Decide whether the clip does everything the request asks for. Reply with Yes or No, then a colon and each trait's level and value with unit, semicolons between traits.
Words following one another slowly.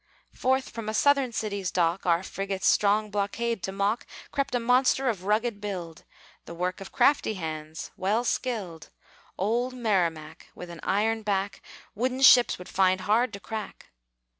No: average, 160 wpm